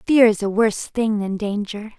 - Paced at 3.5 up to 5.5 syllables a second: Yes, 5.0 syllables/s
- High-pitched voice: Yes, high, 215 Hz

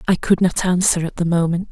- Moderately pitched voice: Yes, medium, 175 Hz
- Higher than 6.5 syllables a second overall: No, 5.8 syllables/s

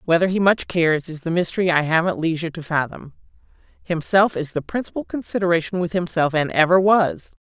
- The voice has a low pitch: No, medium, 170 Hz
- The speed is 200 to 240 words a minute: No, average, 180 wpm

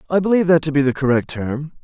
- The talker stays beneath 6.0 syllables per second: No, 7.0 syllables/s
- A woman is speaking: No, male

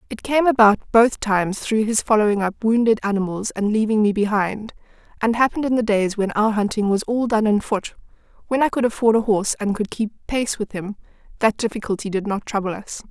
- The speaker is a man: No, female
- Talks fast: Yes, fast, 210 wpm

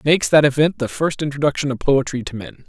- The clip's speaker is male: Yes, male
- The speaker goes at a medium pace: No, fast, 245 wpm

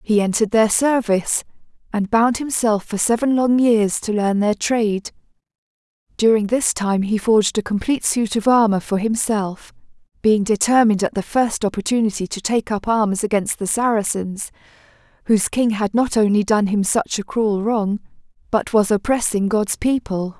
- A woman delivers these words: Yes, female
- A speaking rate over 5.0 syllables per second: No, 4.9 syllables/s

